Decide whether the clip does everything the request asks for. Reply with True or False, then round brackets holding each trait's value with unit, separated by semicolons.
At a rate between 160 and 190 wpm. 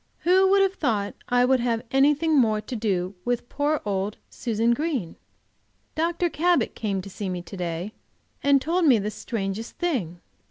True (170 wpm)